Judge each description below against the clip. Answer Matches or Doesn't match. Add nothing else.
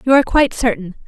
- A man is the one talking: Doesn't match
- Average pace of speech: Doesn't match